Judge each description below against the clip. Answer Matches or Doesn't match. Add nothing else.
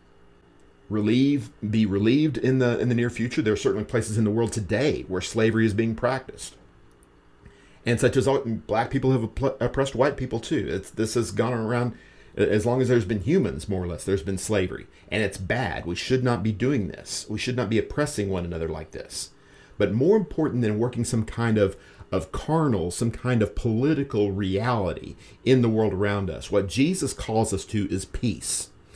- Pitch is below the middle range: Matches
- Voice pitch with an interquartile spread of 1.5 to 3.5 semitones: Doesn't match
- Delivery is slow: Doesn't match